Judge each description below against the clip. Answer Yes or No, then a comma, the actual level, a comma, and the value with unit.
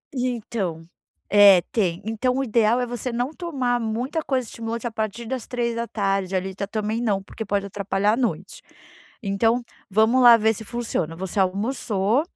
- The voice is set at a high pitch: Yes, high, 220 Hz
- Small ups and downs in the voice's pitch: No, average, 3.4 semitones